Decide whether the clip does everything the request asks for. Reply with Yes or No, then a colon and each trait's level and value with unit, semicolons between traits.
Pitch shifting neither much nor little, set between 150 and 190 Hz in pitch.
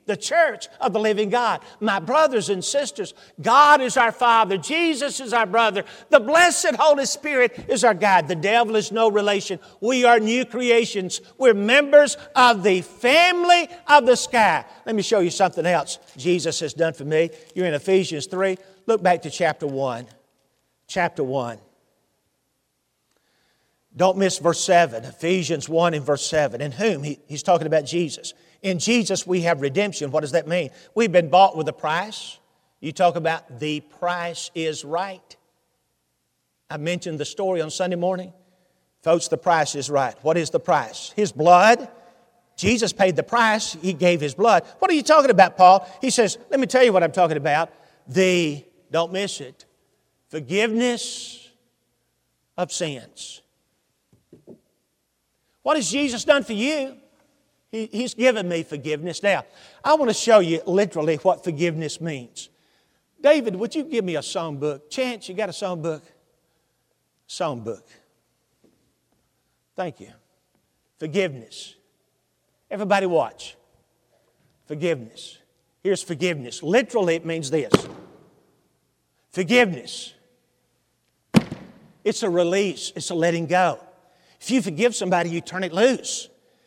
No: wide, 6.1 semitones; medium, 185 Hz